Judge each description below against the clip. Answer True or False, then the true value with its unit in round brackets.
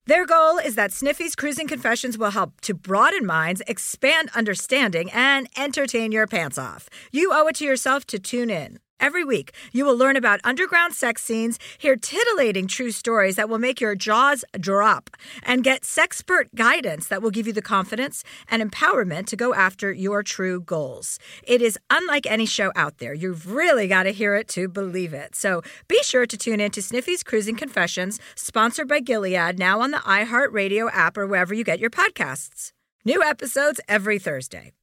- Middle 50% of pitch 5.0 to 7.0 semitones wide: True (5.3 semitones)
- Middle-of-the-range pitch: False (225 Hz)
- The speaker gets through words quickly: False (185 wpm)